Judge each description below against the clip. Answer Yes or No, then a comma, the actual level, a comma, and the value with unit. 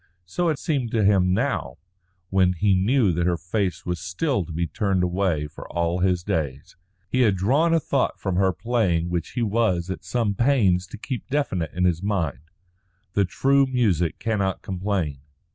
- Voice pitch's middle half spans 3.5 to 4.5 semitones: No, average, 5.0 semitones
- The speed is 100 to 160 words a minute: No, average, 180 wpm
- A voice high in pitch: No, very low, 95 Hz